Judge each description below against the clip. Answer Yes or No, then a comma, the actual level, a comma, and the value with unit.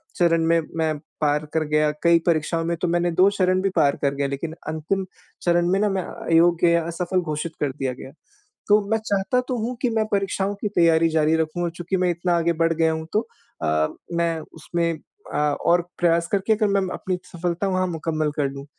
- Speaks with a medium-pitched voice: Yes, medium, 170 Hz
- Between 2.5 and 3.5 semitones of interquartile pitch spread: Yes, average, 2.8 semitones